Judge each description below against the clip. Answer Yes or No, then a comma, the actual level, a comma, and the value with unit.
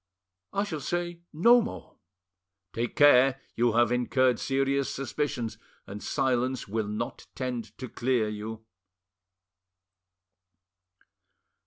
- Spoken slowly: Yes, slow, 105 wpm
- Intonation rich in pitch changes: No, average, 3.4 semitones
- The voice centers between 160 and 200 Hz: No, low, 125 Hz